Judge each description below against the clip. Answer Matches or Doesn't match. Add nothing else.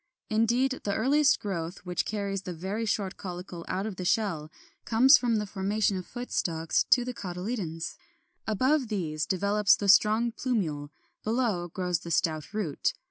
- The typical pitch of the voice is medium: Doesn't match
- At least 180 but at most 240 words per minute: Doesn't match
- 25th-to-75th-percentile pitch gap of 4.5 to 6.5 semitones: Doesn't match